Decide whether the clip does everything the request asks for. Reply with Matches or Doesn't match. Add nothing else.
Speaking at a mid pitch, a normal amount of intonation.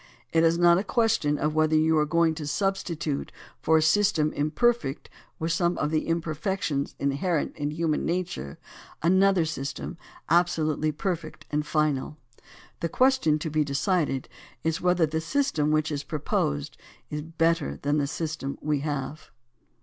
Doesn't match